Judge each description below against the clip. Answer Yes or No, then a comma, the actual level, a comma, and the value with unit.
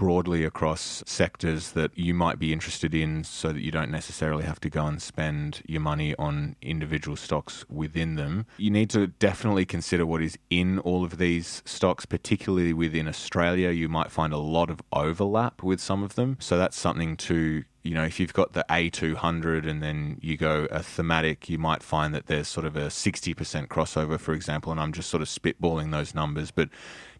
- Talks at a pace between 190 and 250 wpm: Yes, average, 200 wpm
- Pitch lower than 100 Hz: Yes, very low, 80 Hz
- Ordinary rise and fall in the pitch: No, narrow, 2.0 semitones